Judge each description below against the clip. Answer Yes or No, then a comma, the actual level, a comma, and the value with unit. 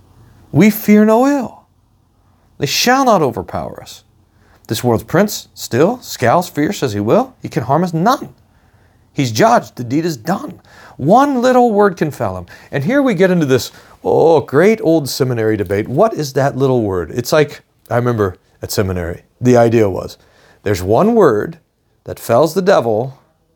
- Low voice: Yes, low, 130 Hz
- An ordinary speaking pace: Yes, average, 170 wpm